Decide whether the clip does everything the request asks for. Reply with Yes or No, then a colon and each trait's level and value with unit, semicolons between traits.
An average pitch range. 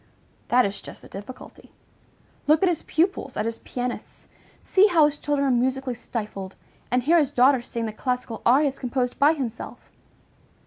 Yes: average, 3.5 semitones